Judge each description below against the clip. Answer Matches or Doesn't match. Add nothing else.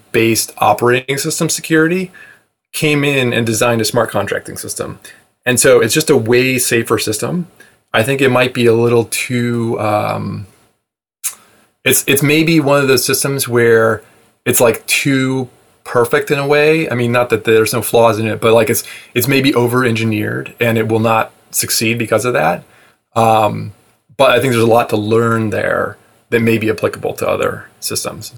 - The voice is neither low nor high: Doesn't match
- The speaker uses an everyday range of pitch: Matches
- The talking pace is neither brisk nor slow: Matches